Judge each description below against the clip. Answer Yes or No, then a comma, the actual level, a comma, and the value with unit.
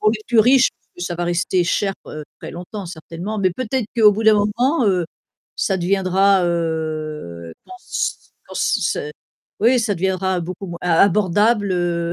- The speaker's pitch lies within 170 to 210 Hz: Yes, high, 190 Hz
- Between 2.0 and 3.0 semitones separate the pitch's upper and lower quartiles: No, average, 3.7 semitones